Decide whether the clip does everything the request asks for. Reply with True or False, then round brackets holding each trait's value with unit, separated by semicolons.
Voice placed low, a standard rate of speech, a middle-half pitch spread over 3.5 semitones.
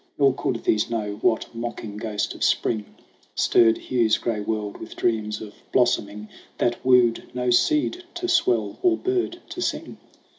True (115 Hz; 160 wpm; 4.1 semitones)